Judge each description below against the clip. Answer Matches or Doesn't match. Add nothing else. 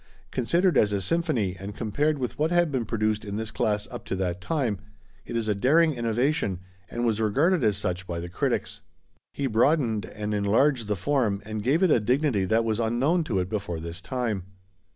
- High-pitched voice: Doesn't match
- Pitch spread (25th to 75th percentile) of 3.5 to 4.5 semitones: Doesn't match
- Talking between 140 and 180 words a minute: Doesn't match